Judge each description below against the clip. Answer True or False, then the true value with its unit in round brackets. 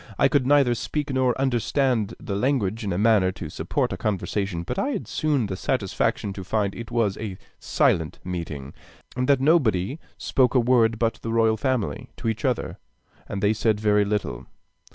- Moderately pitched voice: False (110 Hz)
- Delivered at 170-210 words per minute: True (185 wpm)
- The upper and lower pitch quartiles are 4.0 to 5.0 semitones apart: True (4.4 semitones)